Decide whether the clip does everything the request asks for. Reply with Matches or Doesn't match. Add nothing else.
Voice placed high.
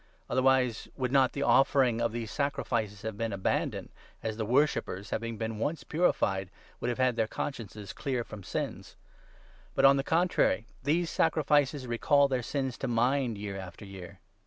Doesn't match